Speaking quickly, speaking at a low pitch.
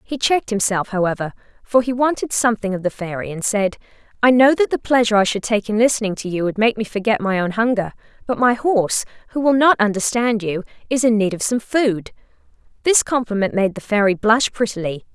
No: fast, 210 wpm; high, 220 Hz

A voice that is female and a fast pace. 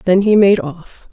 Yes: female; fast, 215 wpm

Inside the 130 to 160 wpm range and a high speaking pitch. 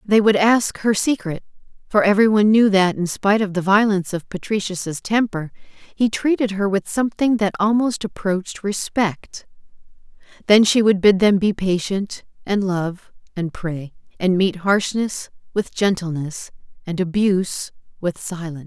Yes: average, 150 wpm; high, 195 Hz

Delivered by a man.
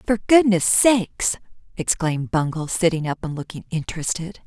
No: female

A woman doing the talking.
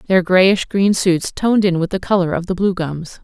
Yes: female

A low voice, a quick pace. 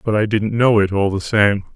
Yes: low, 105 Hz; fast, 275 wpm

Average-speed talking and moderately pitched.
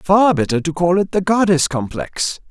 Yes: average, 190 wpm; medium, 175 Hz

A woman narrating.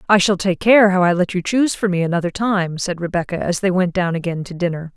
Yes: female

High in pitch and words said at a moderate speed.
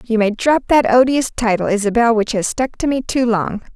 No: high, 235 Hz; fast, 225 wpm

